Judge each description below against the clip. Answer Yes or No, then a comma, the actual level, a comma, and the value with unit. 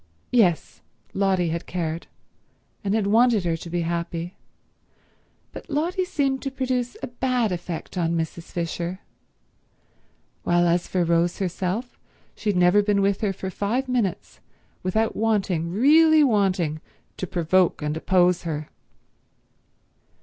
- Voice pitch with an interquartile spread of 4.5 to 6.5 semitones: Yes, average, 4.9 semitones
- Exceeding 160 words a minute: No, slow, 135 wpm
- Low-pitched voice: No, medium, 185 Hz